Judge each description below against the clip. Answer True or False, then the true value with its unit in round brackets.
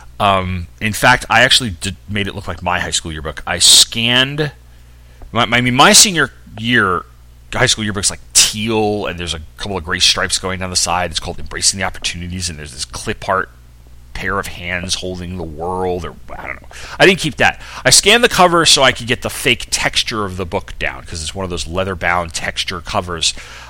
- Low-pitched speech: True (95 Hz)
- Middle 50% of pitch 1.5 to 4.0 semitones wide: False (4.9 semitones)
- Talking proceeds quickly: True (220 wpm)